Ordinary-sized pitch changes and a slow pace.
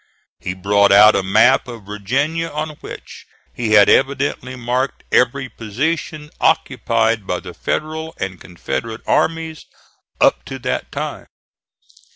No: wide, 6.5 semitones; slow, 130 wpm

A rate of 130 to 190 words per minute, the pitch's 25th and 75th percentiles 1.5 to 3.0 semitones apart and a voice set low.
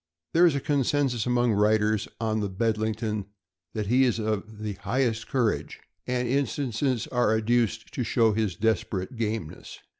Yes: average, 150 wpm; narrow, 2.5 semitones; low, 110 Hz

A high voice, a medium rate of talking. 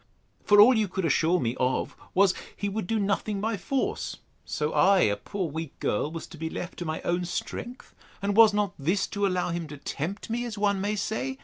No: high, 195 Hz; fast, 220 wpm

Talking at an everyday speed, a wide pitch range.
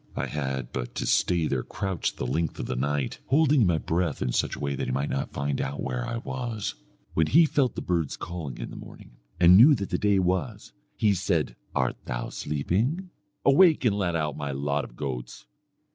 No: fast, 215 wpm; wide, 7.0 semitones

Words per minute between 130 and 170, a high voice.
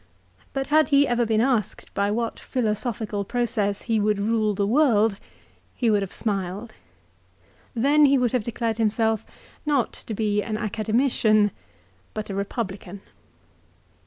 Yes: average, 140 wpm; high, 220 Hz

